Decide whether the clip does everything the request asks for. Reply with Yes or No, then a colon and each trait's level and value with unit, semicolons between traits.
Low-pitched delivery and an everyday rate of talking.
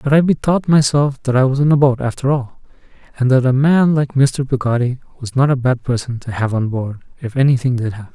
No: low, 130 Hz; fast, 235 wpm